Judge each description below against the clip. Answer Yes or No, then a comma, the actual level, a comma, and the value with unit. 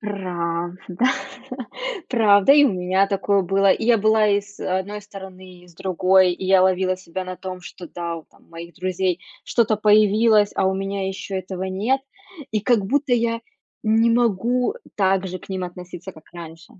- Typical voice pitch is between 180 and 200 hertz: Yes, high, 190 Hz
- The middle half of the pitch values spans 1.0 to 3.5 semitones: Yes, narrow, 2.5 semitones